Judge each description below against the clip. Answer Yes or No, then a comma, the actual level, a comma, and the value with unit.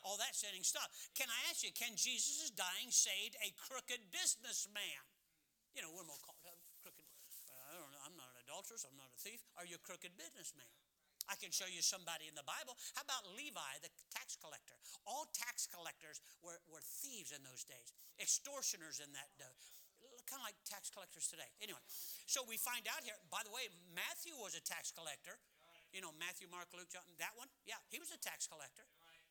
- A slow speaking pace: No, average, 200 wpm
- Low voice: No, medium, 185 Hz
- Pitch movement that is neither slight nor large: No, wide, 5.8 semitones